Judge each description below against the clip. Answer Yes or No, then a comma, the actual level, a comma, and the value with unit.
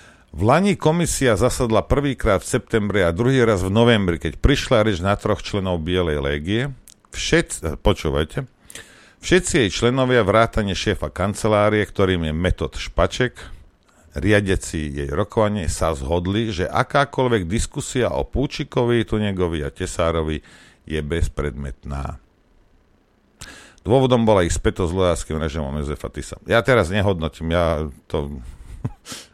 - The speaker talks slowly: No, average, 125 wpm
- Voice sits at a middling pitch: No, very low, 95 Hz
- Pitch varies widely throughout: Yes, wide, 5.9 semitones